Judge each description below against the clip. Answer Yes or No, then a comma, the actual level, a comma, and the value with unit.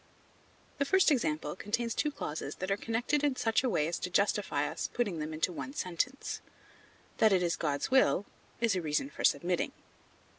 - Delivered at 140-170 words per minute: No, average, 190 wpm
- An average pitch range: No, wide, 7.3 semitones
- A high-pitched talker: Yes, high, 205 Hz